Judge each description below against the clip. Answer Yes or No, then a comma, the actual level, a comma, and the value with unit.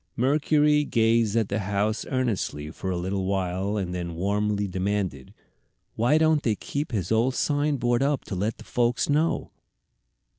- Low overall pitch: Yes, low, 110 Hz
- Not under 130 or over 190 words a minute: Yes, average, 155 wpm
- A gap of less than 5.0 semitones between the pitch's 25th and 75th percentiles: No, wide, 5.5 semitones